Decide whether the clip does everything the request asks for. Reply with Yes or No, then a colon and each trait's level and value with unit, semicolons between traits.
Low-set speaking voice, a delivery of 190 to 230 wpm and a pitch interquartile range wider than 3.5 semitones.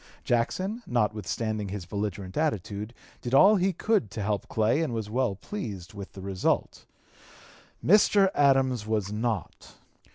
No: low, 110 Hz; slow, 135 wpm; wide, 5.5 semitones